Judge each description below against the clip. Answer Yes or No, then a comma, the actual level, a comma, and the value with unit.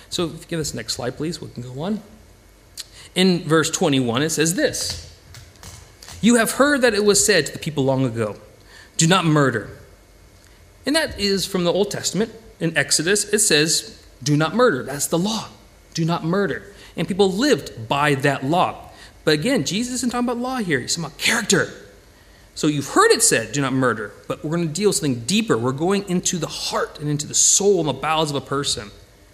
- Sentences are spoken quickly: Yes, fast, 210 wpm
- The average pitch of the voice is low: No, medium, 150 Hz